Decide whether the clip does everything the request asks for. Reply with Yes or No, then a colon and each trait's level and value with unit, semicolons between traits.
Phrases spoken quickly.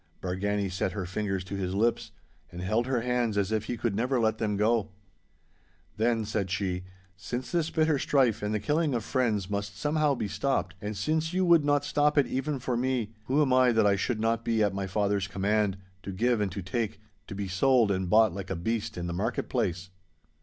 Yes: fast, 215 wpm